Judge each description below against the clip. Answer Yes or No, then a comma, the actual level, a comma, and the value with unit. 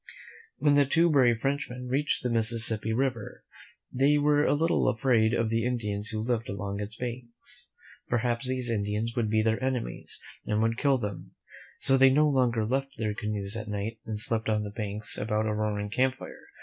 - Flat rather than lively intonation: No, average, 3.3 semitones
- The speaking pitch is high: No, low, 115 Hz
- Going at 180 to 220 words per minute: Yes, average, 190 wpm